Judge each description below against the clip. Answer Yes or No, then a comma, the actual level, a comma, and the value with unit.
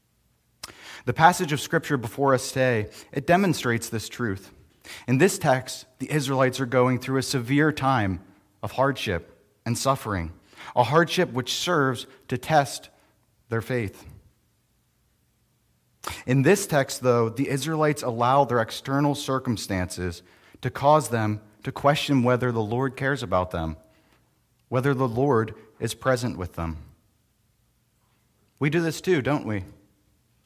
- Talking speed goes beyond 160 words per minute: No, slow, 135 wpm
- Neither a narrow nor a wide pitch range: Yes, average, 4.4 semitones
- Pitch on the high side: No, low, 125 Hz